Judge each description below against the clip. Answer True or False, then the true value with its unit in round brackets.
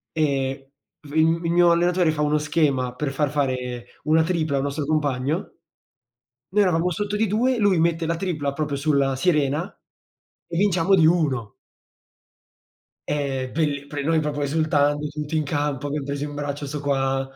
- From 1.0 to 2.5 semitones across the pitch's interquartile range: False (2.9 semitones)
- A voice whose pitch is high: False (150 Hz)